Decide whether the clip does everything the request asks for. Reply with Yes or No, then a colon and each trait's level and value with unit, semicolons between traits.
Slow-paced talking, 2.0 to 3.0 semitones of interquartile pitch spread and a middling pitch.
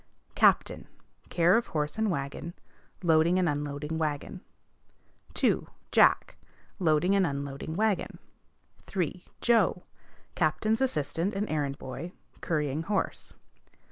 No: slow, 110 wpm; average, 4.4 semitones; medium, 165 Hz